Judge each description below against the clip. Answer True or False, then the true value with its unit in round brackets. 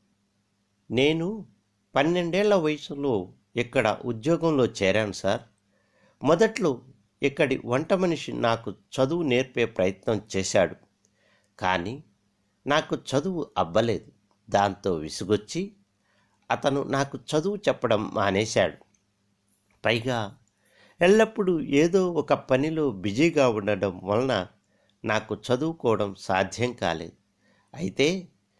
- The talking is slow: False (85 wpm)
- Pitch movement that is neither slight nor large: False (7.0 semitones)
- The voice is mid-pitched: False (120 Hz)